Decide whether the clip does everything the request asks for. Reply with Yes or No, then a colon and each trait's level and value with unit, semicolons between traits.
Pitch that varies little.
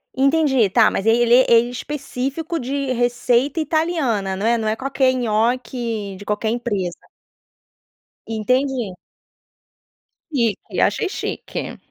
No: average, 3.7 semitones